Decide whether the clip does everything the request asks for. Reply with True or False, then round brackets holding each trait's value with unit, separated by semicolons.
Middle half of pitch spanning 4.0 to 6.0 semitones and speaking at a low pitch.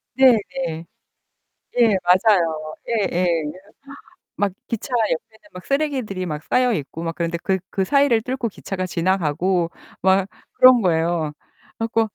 False (5.5 semitones; 190 Hz)